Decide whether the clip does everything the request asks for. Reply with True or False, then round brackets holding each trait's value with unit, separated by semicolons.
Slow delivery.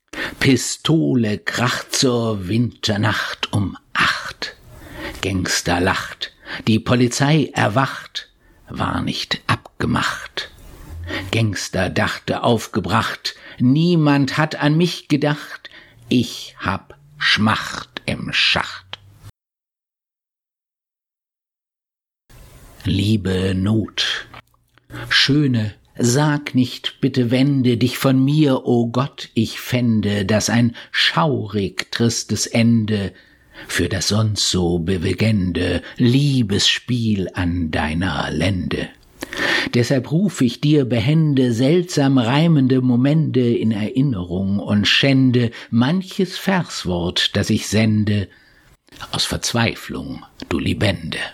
True (90 wpm)